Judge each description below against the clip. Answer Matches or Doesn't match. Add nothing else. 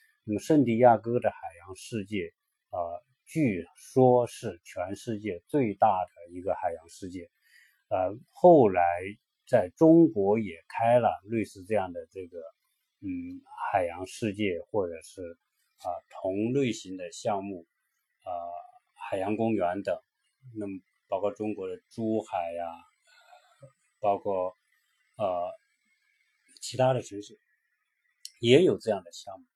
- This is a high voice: Doesn't match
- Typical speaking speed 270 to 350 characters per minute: Doesn't match